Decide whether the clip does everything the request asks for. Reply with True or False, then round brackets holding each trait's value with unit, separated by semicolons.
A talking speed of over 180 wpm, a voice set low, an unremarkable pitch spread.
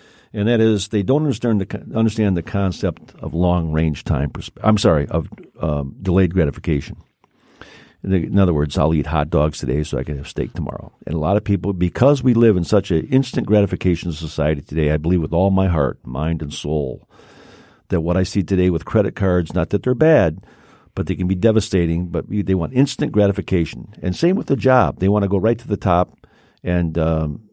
True (205 wpm; 90 Hz; 4.4 semitones)